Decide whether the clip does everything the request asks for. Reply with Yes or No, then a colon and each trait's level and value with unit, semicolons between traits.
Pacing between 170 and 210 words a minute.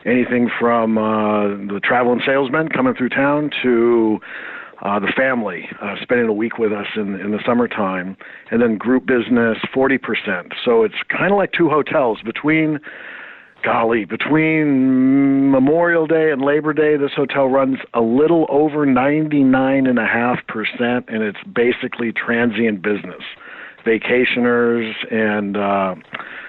No: slow, 135 wpm